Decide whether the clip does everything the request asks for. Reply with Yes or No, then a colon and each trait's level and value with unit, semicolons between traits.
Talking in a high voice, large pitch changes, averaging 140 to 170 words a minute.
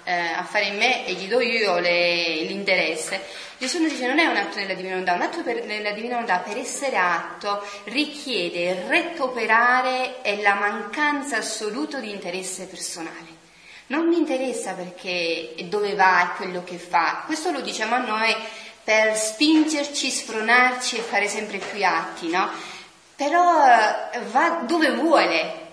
Yes: high, 215 Hz; wide, 5.9 semitones; average, 150 wpm